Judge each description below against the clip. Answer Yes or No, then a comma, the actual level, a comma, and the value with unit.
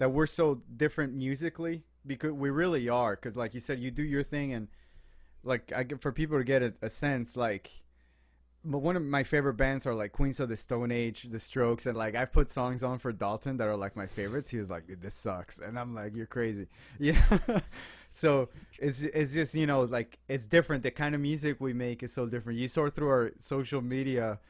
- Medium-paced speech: No, fast, 225 wpm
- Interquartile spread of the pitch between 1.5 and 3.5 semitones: No, average, 4.1 semitones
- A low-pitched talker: Yes, low, 130 Hz